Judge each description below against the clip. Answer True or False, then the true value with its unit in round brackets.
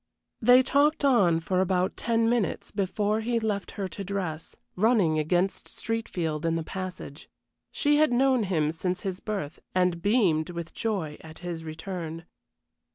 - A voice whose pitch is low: False (185 Hz)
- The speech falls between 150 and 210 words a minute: True (155 wpm)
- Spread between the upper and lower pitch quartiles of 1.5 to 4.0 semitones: False (5.3 semitones)